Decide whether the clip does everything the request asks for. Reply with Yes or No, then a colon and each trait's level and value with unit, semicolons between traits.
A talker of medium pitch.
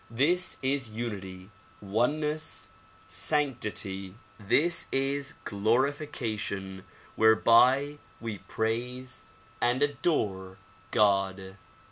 No: low, 115 Hz